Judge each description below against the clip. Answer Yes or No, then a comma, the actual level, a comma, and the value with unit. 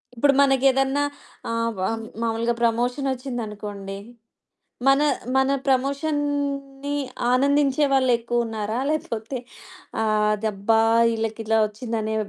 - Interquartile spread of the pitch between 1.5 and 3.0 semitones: No, average, 3.5 semitones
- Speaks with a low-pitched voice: No, high, 240 Hz